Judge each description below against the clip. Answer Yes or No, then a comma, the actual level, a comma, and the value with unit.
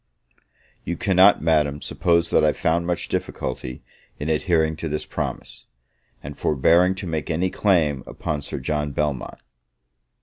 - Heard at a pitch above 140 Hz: No, very low, 80 Hz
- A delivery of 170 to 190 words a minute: No, average, 140 wpm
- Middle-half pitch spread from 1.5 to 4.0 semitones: Yes, average, 2.7 semitones